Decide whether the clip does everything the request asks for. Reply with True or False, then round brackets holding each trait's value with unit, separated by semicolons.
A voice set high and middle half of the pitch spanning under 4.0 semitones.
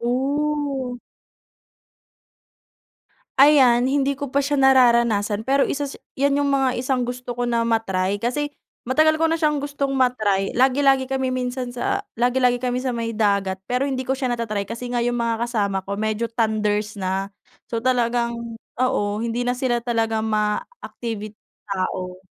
True (245 Hz; 3.2 semitones)